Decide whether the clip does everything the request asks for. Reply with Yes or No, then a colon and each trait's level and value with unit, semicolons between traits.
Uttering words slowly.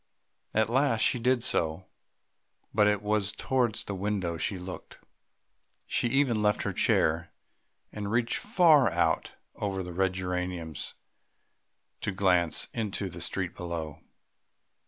Yes: slow, 130 wpm